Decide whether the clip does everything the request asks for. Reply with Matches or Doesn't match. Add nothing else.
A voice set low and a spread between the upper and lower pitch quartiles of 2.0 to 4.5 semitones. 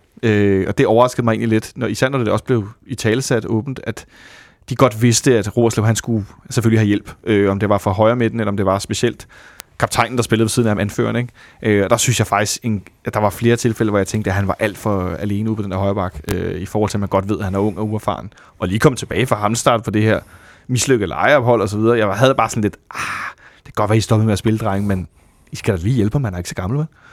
Matches